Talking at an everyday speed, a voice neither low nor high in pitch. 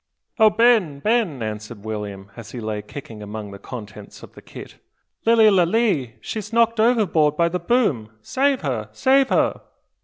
Yes: average, 160 wpm; medium, 150 Hz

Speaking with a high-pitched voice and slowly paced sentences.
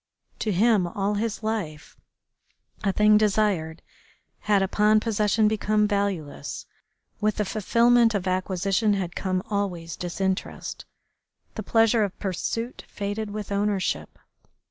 Yes: high, 205 Hz; slow, 120 wpm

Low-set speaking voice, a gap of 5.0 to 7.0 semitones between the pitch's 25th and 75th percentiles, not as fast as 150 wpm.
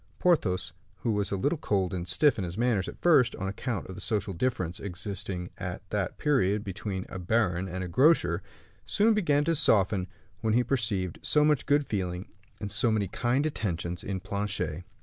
No: low, 100 Hz; average, 5.3 semitones; average, 190 wpm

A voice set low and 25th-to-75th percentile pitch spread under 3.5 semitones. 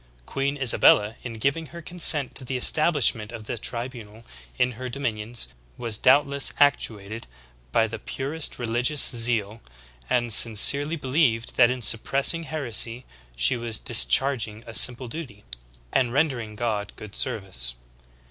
No: low, 120 Hz; average, 3.8 semitones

